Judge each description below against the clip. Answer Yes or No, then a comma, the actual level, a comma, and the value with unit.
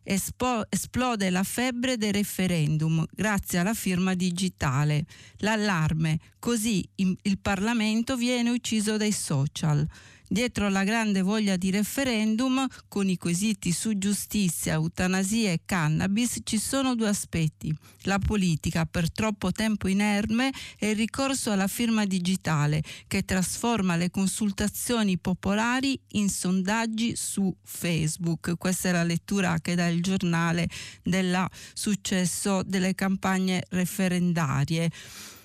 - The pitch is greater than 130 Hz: Yes, high, 190 Hz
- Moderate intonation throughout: Yes, average, 3.8 semitones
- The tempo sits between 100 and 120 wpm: Yes, slow, 115 wpm